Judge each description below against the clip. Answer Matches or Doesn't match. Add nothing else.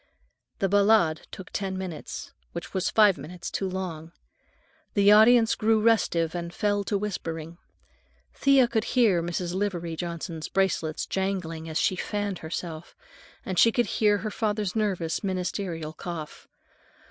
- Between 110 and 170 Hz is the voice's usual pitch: Doesn't match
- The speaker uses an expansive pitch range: Doesn't match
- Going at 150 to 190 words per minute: Doesn't match